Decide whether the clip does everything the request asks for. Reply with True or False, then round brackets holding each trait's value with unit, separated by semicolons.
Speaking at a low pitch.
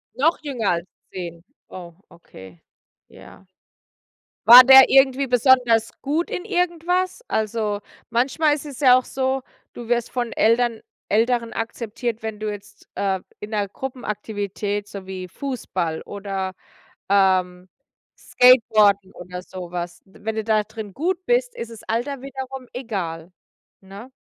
False (225 Hz)